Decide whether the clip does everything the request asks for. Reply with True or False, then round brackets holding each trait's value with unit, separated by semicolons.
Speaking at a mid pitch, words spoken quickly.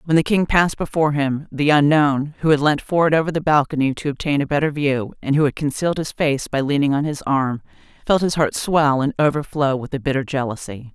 True (145 Hz; 225 wpm)